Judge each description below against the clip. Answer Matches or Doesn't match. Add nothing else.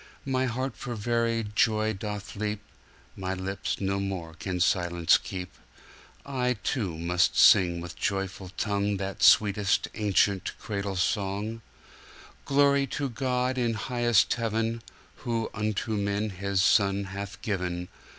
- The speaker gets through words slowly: Matches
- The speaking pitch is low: Matches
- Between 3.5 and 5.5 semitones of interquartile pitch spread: Doesn't match